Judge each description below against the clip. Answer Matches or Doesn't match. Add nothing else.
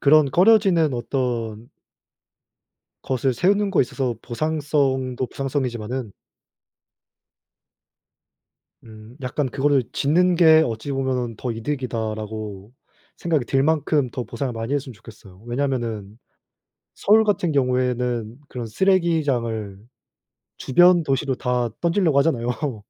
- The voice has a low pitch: Matches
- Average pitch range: Matches